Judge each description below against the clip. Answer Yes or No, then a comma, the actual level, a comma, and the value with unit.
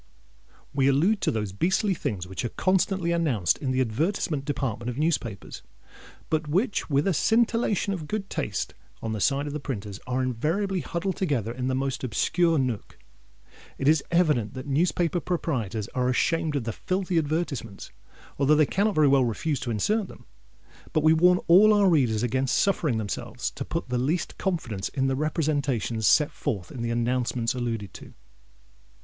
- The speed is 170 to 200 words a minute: Yes, average, 175 wpm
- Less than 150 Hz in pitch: Yes, medium, 140 Hz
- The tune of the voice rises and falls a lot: Yes, wide, 6.0 semitones